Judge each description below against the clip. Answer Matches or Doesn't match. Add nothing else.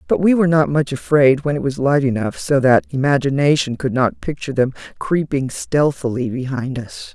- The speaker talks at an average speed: Matches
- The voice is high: Doesn't match